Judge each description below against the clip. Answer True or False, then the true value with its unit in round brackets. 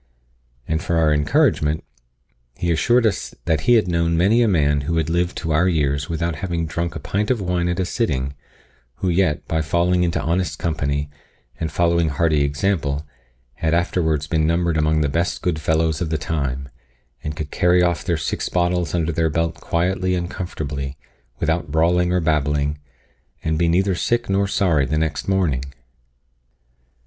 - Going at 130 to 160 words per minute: False (175 wpm)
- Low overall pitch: True (80 Hz)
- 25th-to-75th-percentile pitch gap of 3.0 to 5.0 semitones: False (2.6 semitones)